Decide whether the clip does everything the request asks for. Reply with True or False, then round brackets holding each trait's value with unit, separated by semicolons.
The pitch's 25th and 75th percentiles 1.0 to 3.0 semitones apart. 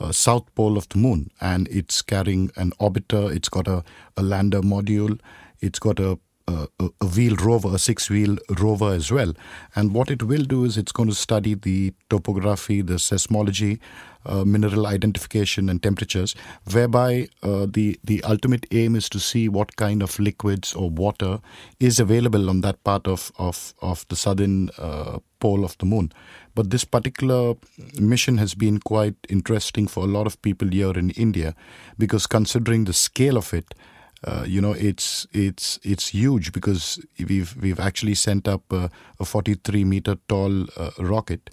True (2.5 semitones)